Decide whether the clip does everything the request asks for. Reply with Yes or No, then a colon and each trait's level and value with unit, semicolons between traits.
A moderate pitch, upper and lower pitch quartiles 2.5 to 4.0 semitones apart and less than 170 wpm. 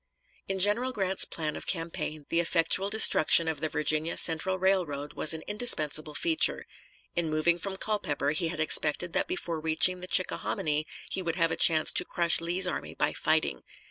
No: medium, 170 Hz; average, 3.3 semitones; average, 175 wpm